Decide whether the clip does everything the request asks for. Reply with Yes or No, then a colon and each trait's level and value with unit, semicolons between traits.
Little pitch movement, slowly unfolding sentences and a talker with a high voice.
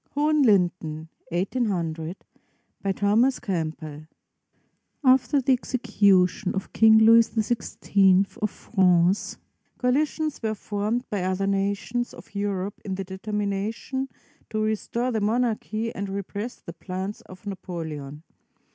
No: average, 3.6 semitones; slow, 110 wpm; high, 200 Hz